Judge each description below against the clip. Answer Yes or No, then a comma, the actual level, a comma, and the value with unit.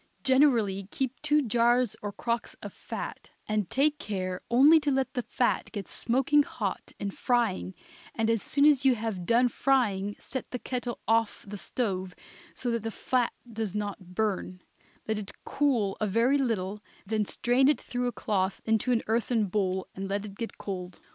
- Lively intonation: No, average, 4.0 semitones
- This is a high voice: Yes, high, 225 Hz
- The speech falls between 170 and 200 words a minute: Yes, average, 180 wpm